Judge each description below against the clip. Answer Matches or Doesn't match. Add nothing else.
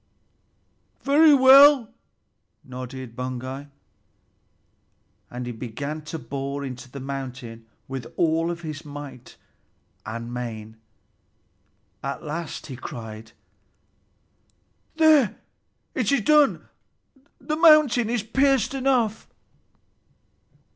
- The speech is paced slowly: Matches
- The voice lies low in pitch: Doesn't match